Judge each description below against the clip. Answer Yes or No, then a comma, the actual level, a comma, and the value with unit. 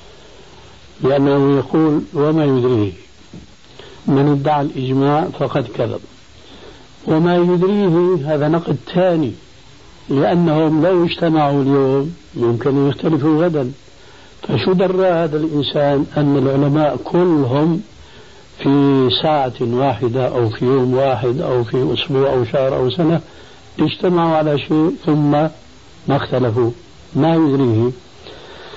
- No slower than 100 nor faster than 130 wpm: Yes, average, 110 wpm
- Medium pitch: Yes, medium, 145 Hz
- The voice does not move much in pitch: No, average, 3.4 semitones